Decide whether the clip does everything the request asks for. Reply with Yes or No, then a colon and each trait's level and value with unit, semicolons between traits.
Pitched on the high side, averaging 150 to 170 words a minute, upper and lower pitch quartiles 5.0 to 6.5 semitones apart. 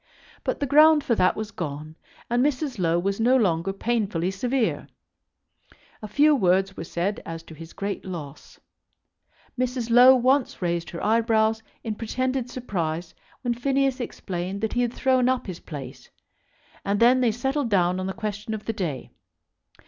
Yes: high, 220 Hz; average, 165 wpm; wide, 5.5 semitones